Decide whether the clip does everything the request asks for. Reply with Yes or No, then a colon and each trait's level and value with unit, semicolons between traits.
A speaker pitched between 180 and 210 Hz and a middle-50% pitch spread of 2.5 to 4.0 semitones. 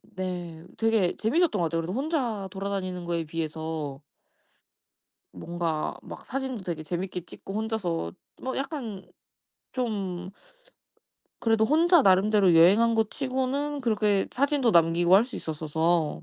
No: high, 190 Hz; average, 5.2 semitones